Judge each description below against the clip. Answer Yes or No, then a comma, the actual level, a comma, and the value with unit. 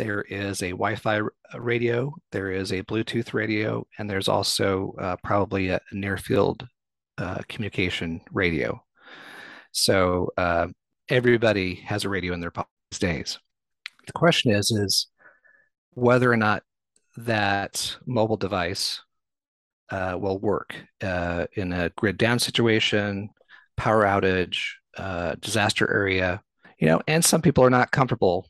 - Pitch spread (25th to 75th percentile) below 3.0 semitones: No, average, 3.3 semitones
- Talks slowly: Yes, slow, 130 wpm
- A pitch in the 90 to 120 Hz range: Yes, low, 100 Hz